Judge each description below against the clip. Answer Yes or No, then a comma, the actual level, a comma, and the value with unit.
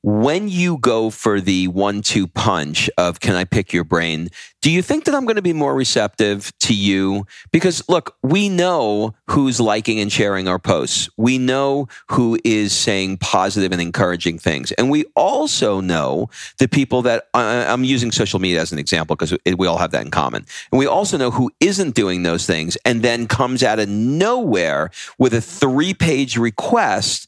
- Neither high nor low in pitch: No, low, 115 Hz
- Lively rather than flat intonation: Yes, wide, 5.8 semitones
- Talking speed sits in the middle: Yes, average, 190 wpm